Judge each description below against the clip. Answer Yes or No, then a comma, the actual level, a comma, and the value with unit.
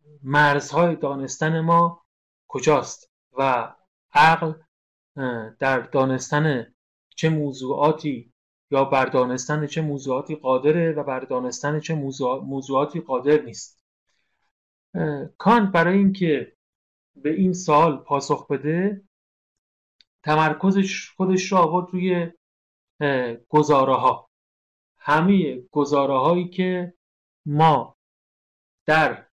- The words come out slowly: Yes, slow, 90 wpm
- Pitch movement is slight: No, average, 4.1 semitones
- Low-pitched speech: No, medium, 150 Hz